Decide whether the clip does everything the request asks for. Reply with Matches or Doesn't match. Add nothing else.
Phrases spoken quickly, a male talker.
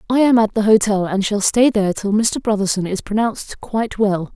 Doesn't match